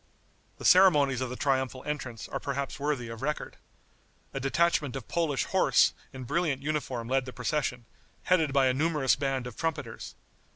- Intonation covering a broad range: No, average, 2.9 semitones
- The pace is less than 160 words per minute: No, average, 165 wpm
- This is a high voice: No, low, 135 Hz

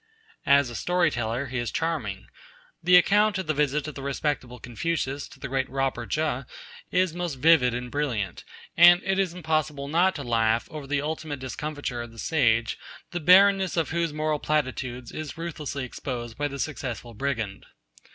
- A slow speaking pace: No, average, 175 wpm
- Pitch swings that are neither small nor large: Yes, average, 4.6 semitones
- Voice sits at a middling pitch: Yes, medium, 145 Hz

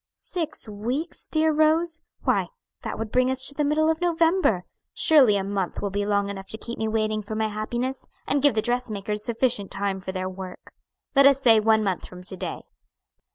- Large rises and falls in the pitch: Yes, wide, 5.8 semitones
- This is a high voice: Yes, high, 220 Hz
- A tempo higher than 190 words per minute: Yes, average, 200 wpm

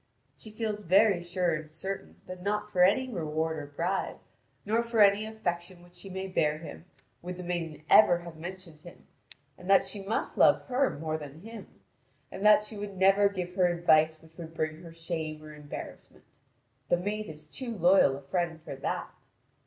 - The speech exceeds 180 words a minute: Yes, average, 190 wpm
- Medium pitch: Yes, medium, 175 Hz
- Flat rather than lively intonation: No, average, 4.0 semitones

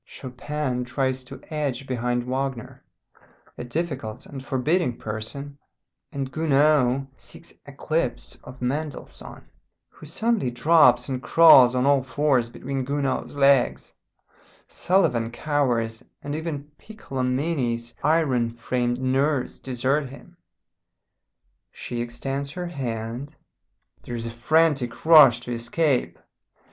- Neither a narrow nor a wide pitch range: Yes, average, 3.3 semitones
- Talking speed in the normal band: No, slow, 110 wpm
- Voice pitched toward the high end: No, low, 135 Hz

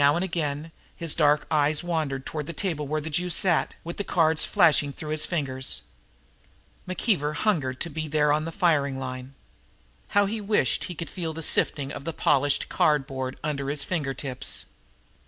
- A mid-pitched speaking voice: Yes, medium, 150 Hz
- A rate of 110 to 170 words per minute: No, average, 180 wpm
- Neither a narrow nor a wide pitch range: Yes, average, 3.1 semitones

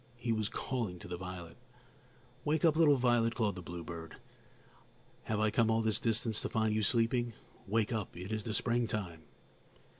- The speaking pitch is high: No, low, 110 Hz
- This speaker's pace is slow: No, average, 175 wpm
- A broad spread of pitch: No, average, 3.7 semitones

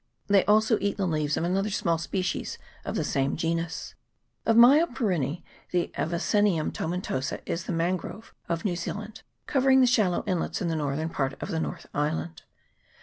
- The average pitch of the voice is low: No, medium, 175 Hz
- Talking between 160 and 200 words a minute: Yes, average, 170 wpm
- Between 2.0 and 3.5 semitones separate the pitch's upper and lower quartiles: No, average, 4.4 semitones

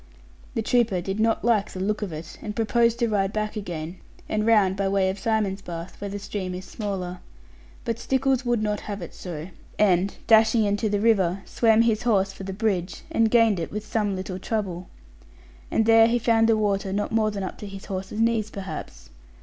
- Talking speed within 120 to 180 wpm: No, fast, 205 wpm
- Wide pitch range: No, average, 2.8 semitones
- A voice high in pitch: Yes, high, 205 Hz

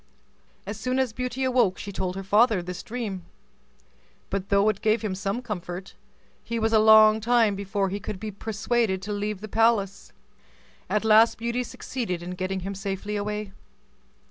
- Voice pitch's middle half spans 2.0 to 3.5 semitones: Yes, narrow, 2.6 semitones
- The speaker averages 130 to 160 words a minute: No, average, 170 wpm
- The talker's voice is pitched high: Yes, high, 210 Hz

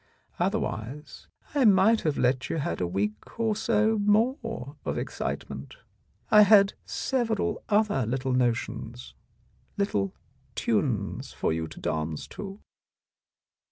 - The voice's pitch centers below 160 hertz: No, medium, 185 Hz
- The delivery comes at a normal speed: No, slow, 120 wpm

